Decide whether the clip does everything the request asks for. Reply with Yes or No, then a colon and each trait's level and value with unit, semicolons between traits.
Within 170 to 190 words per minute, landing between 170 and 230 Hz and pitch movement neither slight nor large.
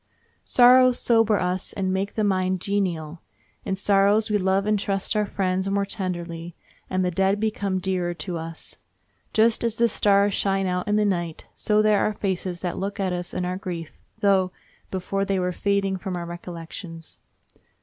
No: average, 180 wpm; high, 190 Hz; narrow, 2.1 semitones